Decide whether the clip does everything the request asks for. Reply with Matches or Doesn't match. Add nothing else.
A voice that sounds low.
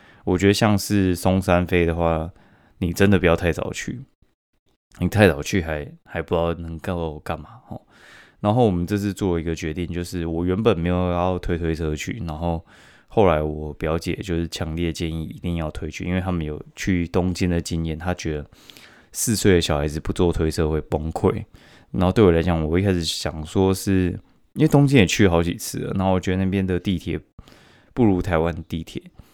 Matches